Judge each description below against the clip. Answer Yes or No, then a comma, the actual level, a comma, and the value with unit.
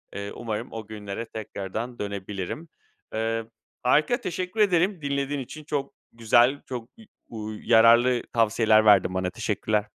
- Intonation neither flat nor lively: Yes, average, 4.7 semitones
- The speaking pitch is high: No, low, 115 Hz